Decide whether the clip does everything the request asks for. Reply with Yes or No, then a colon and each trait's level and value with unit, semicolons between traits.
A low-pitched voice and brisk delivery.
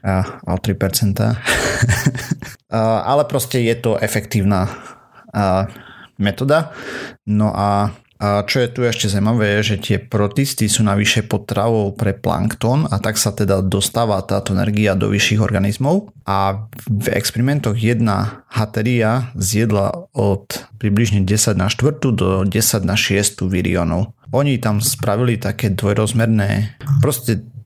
No: low, 110 Hz; average, 125 wpm